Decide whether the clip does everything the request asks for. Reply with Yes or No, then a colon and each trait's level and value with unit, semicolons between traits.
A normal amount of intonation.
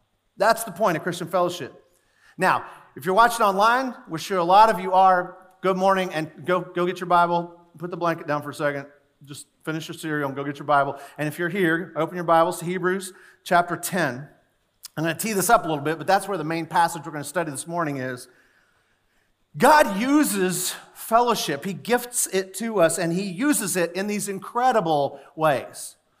Yes: average, 3.5 semitones